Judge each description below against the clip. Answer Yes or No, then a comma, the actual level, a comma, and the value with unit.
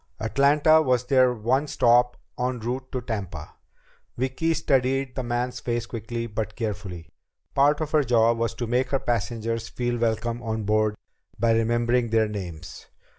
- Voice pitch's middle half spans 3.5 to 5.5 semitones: No, narrow, 2.4 semitones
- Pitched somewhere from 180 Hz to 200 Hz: No, low, 120 Hz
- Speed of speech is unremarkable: Yes, average, 155 wpm